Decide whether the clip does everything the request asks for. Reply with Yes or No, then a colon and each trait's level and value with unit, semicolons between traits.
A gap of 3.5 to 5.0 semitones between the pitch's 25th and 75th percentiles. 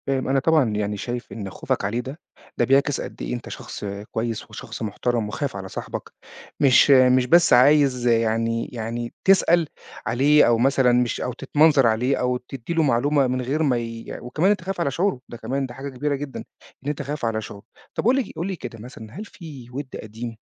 Yes: average, 3.9 semitones